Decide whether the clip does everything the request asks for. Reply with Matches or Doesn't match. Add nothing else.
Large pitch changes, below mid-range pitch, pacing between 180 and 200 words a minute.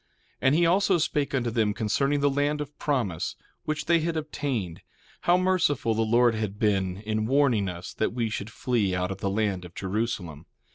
Matches